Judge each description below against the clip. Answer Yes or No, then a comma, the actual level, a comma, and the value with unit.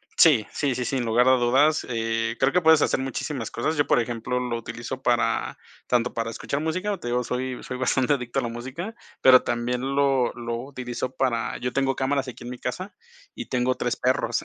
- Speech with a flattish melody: Yes, narrow, 2.3 semitones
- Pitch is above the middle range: No, low, 125 Hz